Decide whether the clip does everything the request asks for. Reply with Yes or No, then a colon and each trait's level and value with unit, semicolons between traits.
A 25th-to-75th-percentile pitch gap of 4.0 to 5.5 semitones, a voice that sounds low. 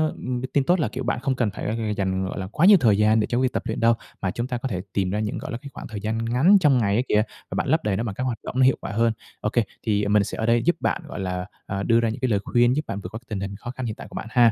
No: average, 3.5 semitones; low, 115 Hz